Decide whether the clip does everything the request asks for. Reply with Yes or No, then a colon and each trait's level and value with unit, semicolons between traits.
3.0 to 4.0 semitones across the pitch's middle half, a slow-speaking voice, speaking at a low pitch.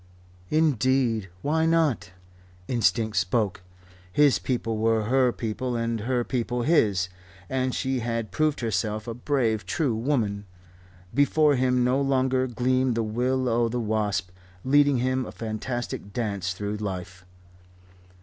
Yes: average, 3.3 semitones; slow, 130 wpm; low, 120 Hz